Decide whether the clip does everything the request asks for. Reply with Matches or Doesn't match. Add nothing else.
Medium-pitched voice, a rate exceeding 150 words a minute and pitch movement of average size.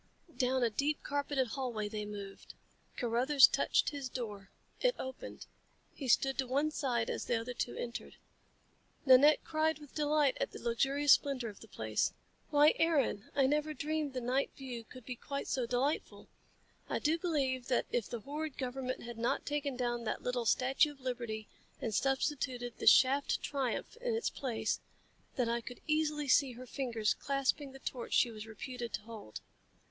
Doesn't match